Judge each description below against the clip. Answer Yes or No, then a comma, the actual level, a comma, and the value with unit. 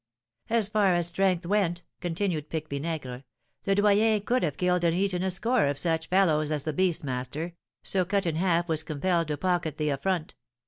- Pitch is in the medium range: Yes, medium, 175 Hz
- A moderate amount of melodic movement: Yes, average, 3.7 semitones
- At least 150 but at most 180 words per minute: No, average, 190 wpm